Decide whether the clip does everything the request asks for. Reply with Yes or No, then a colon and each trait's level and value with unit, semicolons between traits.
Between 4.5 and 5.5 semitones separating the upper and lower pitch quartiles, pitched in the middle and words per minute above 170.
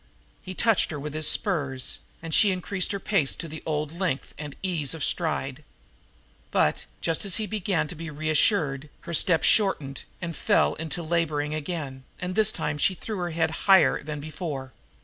No: average, 3.6 semitones; medium, 160 Hz; average, 185 wpm